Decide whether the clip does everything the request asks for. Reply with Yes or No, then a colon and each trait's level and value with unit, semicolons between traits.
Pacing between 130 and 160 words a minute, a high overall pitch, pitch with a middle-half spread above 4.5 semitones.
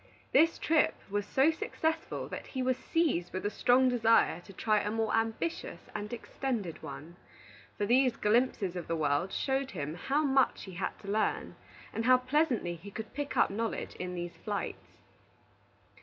No: average, 170 wpm; high, 225 Hz; wide, 5.6 semitones